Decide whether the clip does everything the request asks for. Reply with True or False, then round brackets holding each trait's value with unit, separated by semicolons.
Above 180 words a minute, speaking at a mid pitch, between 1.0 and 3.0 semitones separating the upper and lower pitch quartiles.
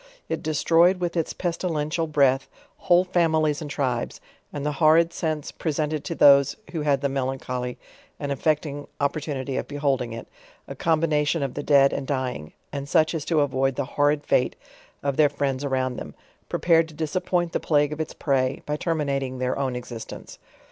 False (175 wpm; 145 Hz; 2.7 semitones)